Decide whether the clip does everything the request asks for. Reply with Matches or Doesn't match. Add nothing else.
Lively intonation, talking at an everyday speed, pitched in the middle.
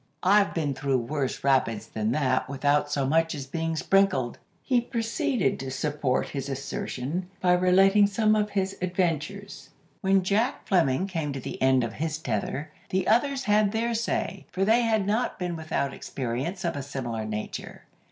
Matches